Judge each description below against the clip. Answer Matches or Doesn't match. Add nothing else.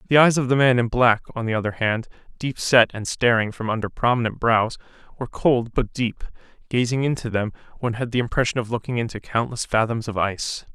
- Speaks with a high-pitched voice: Doesn't match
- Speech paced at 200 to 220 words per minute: Matches